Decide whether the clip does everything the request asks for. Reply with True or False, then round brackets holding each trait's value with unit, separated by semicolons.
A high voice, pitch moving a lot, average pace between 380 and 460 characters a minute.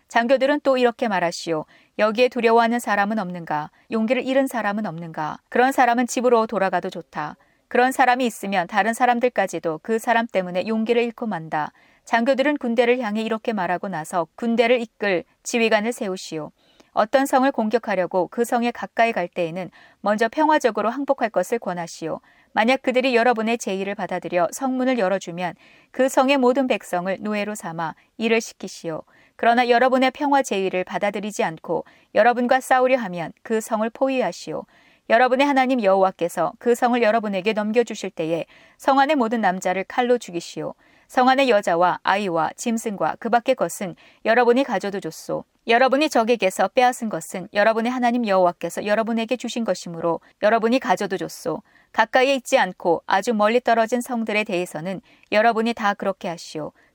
False (225 Hz; 5.0 semitones; 385 characters per minute)